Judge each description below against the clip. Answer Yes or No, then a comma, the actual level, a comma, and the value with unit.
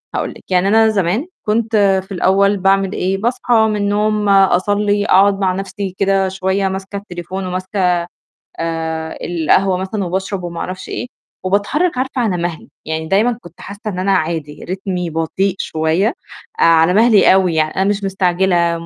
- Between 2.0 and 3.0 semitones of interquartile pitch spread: Yes, narrow, 2.4 semitones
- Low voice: No, high, 190 Hz